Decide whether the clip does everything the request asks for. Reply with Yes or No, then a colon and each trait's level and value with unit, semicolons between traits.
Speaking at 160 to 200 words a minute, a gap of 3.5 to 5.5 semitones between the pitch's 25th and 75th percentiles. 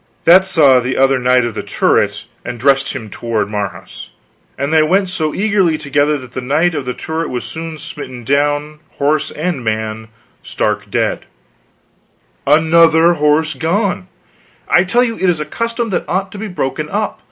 Yes: average, 175 wpm; average, 5.2 semitones